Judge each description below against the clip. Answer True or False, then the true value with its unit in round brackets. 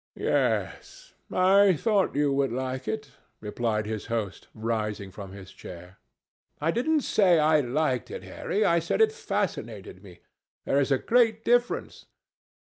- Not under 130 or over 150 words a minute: True (145 wpm)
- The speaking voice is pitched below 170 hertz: True (140 Hz)